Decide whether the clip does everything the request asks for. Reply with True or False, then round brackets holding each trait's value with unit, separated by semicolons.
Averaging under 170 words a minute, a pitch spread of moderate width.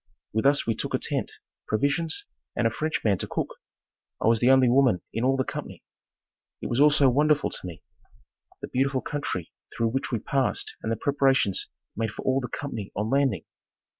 False (195 wpm; 3.8 semitones)